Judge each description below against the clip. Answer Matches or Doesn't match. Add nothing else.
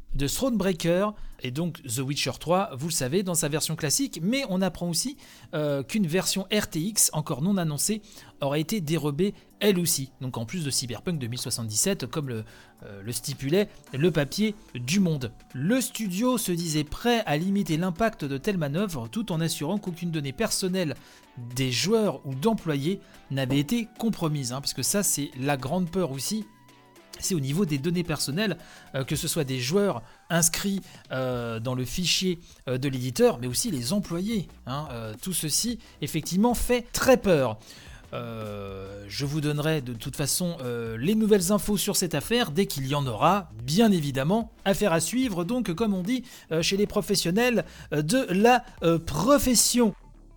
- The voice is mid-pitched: Matches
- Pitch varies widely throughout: Matches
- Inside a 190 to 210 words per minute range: Doesn't match